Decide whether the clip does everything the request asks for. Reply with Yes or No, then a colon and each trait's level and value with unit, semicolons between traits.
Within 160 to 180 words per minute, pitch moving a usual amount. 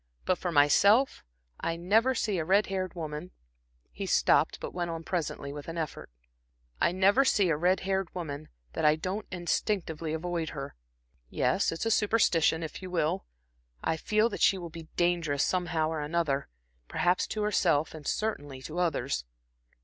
Yes: average, 170 wpm; average, 3.4 semitones